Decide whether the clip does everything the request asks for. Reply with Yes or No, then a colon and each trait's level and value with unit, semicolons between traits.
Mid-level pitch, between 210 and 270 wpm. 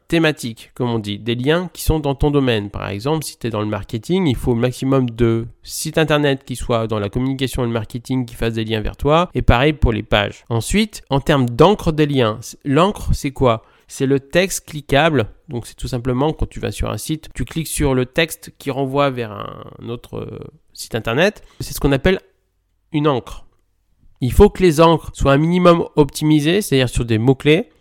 No: low, 130 Hz; average, 215 wpm